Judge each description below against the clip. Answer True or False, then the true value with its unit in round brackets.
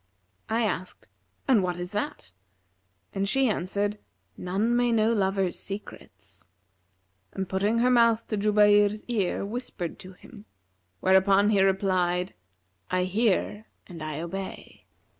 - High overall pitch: True (200 Hz)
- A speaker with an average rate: False (130 wpm)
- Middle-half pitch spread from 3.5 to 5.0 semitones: False (2.9 semitones)